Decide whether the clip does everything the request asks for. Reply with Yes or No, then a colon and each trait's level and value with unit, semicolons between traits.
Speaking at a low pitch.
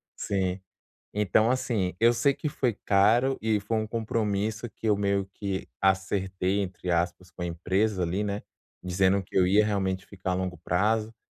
Yes: low, 100 Hz